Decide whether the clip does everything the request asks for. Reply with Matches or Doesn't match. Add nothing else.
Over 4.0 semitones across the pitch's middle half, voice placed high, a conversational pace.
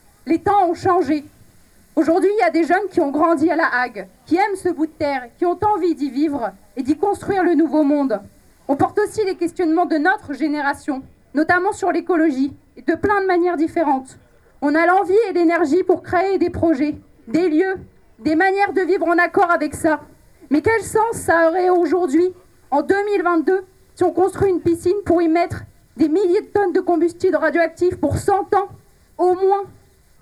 Doesn't match